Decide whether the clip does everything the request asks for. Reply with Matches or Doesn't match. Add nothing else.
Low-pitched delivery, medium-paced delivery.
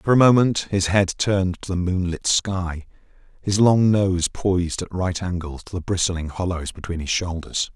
Matches